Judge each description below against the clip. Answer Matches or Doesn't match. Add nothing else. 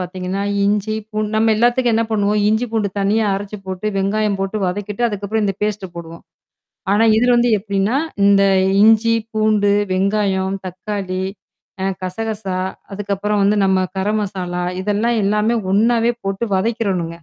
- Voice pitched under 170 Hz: Doesn't match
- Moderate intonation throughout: Doesn't match